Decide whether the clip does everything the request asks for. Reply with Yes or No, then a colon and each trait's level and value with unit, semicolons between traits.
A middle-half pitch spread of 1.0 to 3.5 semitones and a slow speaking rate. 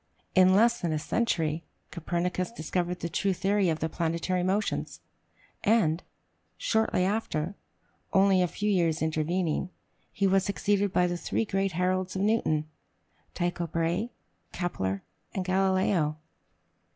Yes: average, 2.7 semitones; slow, 130 wpm